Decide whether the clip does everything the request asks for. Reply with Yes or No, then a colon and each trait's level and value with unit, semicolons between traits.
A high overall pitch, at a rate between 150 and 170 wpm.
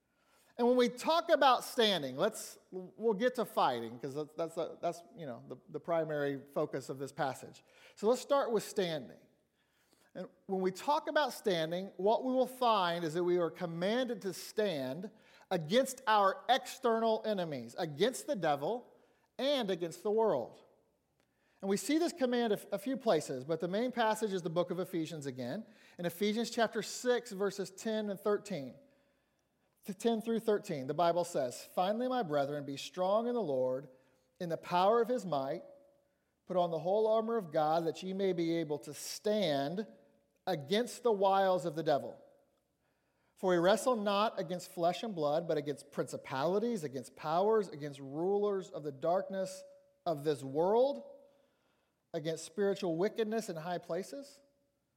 Yes: high, 195 Hz; average, 165 wpm